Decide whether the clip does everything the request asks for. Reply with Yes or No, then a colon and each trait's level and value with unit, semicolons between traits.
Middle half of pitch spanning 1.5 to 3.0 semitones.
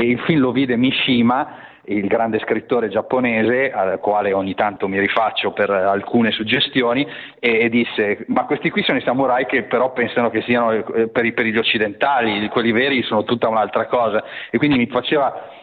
Yes: narrow, 2.5 semitones